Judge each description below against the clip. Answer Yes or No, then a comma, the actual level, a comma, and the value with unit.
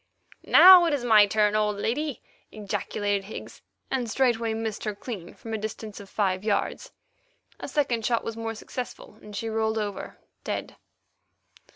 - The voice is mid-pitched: No, high, 220 Hz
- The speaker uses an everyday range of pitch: No, narrow, 2.1 semitones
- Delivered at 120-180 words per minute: Yes, average, 160 wpm